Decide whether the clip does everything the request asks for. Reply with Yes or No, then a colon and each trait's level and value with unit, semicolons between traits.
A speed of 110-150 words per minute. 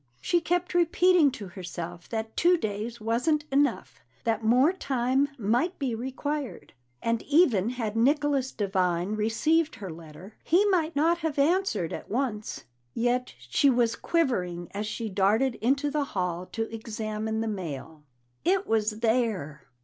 Yes: average, 145 wpm